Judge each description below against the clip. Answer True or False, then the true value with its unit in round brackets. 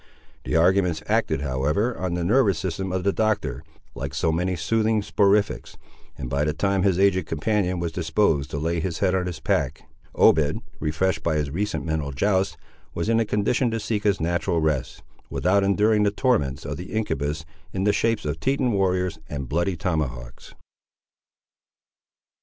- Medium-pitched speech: False (90 Hz)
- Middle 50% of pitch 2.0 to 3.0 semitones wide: False (4.5 semitones)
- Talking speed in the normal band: True (170 wpm)